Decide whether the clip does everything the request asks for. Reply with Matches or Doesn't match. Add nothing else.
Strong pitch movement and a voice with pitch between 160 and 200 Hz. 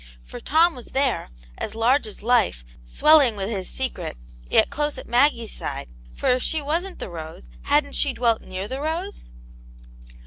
Doesn't match